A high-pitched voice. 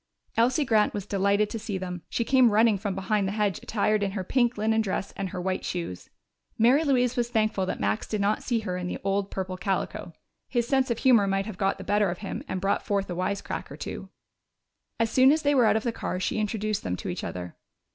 Yes: high, 205 Hz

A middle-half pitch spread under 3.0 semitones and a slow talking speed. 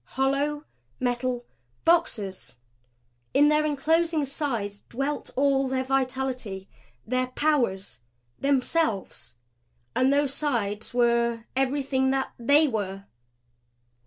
No: average, 3.3 semitones; slow, 95 wpm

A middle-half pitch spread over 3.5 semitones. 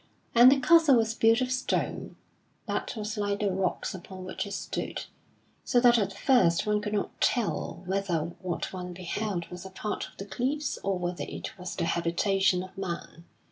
Yes: average, 3.9 semitones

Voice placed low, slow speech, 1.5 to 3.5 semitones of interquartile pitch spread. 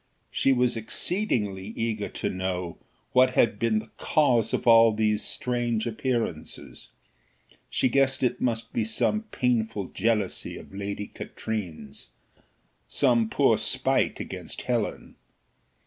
Yes: low, 115 Hz; slow, 120 wpm; average, 2.9 semitones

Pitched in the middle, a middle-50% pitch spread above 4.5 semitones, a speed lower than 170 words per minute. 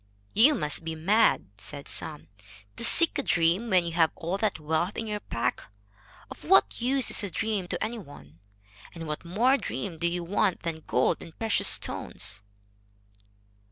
No: medium, 175 Hz; average, 5.3 semitones; average, 175 wpm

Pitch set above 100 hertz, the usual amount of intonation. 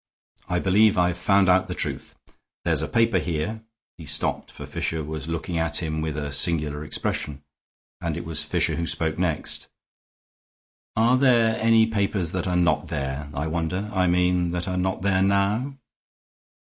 No: very low, 90 Hz; average, 3.9 semitones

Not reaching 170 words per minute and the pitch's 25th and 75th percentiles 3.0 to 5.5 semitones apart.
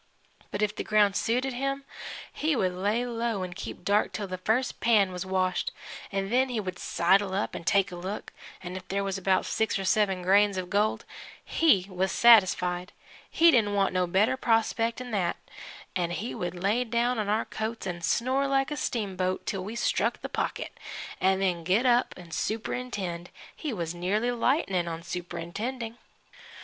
No: average, 185 wpm; average, 4.1 semitones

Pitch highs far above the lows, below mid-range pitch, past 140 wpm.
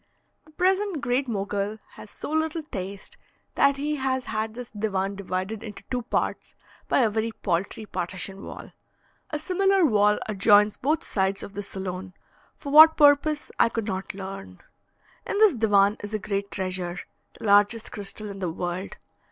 No: wide, 5.9 semitones; high, 210 Hz; average, 165 wpm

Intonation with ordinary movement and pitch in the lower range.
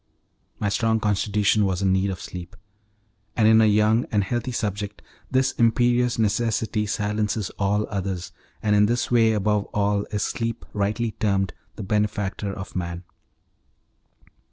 No: narrow, 2.1 semitones; low, 105 Hz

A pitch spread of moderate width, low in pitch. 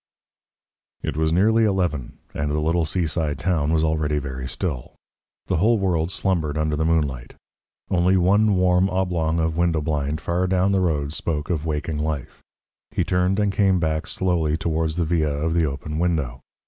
Yes: average, 3.0 semitones; very low, 80 Hz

